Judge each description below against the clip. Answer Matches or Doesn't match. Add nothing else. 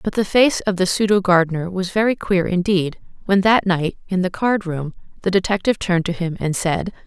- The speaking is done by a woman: Matches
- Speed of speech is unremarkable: Doesn't match